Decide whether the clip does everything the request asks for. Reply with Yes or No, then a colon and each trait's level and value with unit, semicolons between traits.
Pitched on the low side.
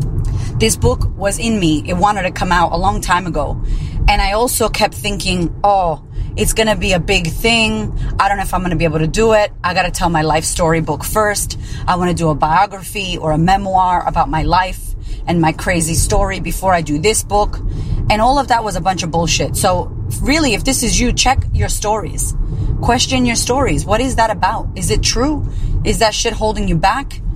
No: medium, 165 Hz